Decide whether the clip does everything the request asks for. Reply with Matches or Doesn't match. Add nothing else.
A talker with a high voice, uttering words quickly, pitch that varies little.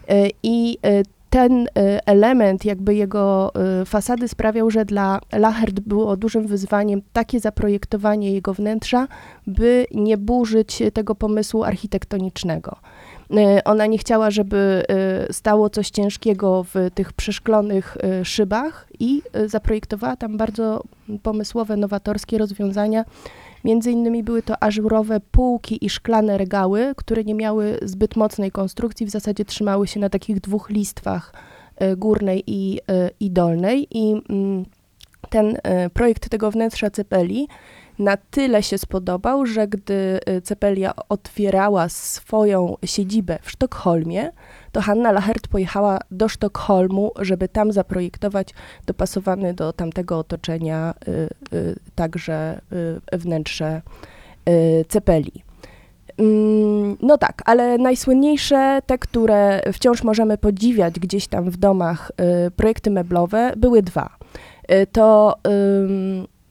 Doesn't match